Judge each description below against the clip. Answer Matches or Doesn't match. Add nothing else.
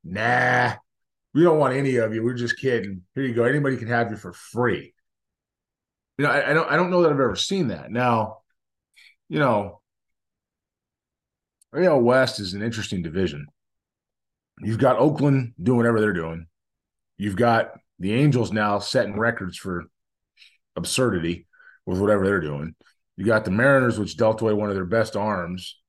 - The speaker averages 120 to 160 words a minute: Doesn't match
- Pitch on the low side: Matches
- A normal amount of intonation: Matches